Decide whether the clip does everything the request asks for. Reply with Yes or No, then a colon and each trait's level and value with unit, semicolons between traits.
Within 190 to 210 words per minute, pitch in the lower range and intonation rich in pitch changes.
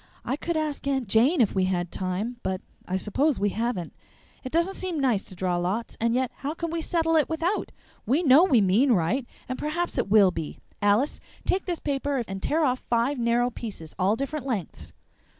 No: fast, 205 wpm; high, 245 Hz; wide, 7.1 semitones